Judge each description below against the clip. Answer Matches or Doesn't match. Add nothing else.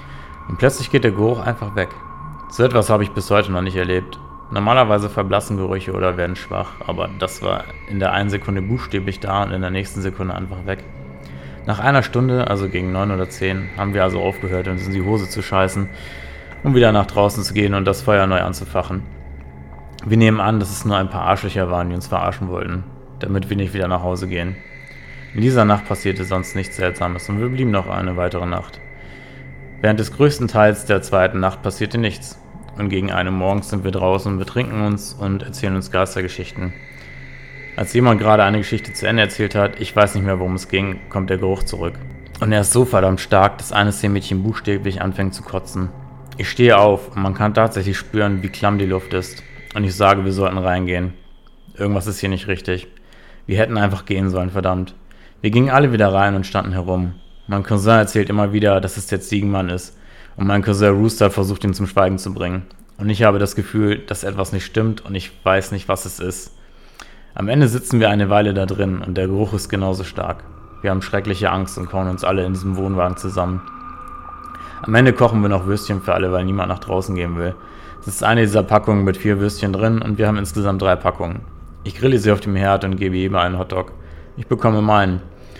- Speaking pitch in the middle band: Doesn't match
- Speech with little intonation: Matches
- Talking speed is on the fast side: Matches